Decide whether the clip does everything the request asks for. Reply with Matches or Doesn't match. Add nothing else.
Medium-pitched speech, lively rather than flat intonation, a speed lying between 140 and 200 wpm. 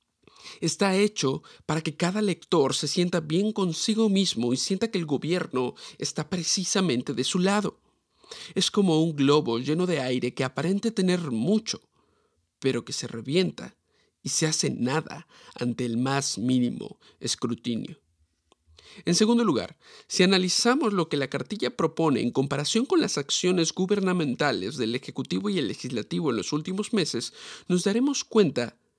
Matches